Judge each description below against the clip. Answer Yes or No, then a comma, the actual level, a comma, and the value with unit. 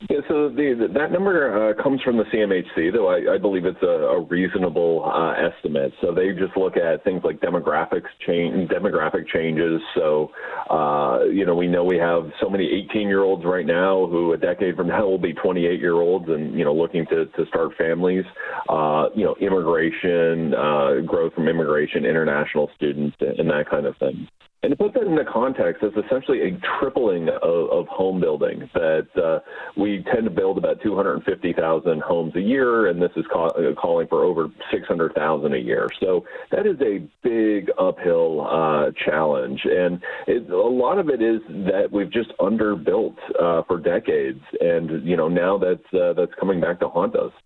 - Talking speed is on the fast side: No, average, 180 wpm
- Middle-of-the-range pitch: Yes, medium, 145 Hz